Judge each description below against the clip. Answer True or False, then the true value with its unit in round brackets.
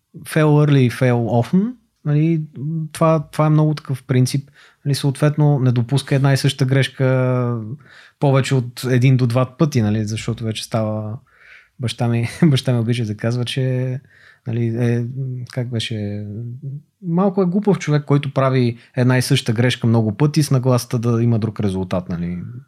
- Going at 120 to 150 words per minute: False (160 wpm)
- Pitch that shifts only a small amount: False (3.4 semitones)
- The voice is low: True (130 Hz)